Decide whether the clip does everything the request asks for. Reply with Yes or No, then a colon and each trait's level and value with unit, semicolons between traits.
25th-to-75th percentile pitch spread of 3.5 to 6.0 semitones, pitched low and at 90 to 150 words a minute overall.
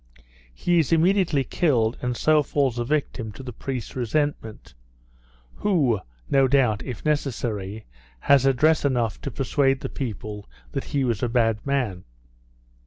Yes: average, 4.4 semitones; low, 130 Hz; average, 145 wpm